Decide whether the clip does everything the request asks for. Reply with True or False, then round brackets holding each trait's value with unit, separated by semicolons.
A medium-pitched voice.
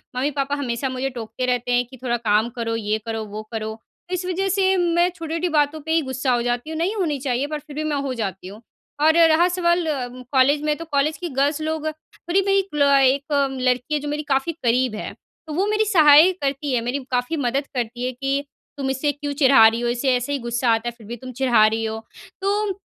False (275 Hz)